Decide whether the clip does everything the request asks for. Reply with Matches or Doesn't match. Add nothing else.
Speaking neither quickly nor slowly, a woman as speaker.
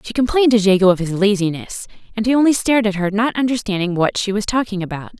Doesn't match